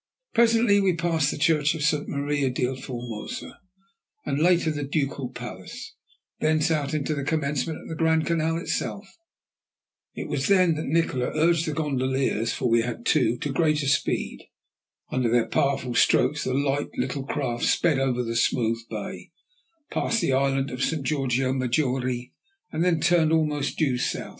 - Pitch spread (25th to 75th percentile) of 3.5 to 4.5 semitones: Yes, average, 3.8 semitones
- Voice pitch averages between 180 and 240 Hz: No, medium, 145 Hz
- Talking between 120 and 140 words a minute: No, average, 160 wpm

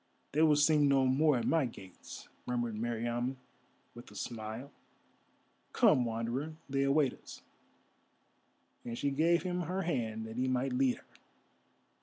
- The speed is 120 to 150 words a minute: Yes, average, 145 wpm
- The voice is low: Yes, low, 130 Hz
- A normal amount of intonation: Yes, average, 3.9 semitones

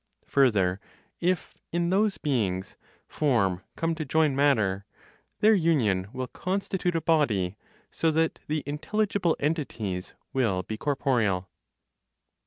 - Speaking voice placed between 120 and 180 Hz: Yes, medium, 140 Hz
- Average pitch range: No, wide, 8.3 semitones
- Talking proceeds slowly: Yes, slow, 115 wpm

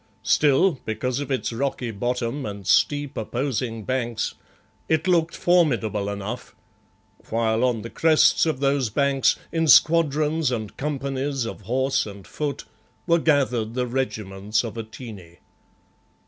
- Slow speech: Yes, slow, 130 wpm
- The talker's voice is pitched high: No, low, 130 Hz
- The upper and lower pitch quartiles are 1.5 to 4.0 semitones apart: No, average, 4.5 semitones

